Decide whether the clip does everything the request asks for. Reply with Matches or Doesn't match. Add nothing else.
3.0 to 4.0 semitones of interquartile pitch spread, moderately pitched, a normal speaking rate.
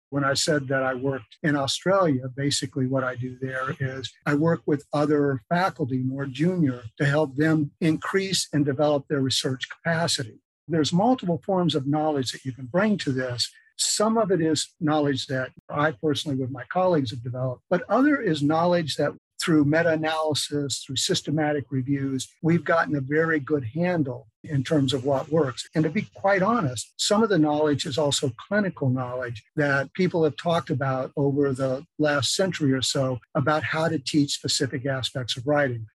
Matches